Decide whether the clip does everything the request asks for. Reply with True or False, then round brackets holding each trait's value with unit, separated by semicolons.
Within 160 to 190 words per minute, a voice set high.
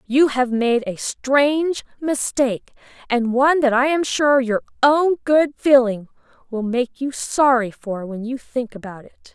True (165 wpm; 255 Hz)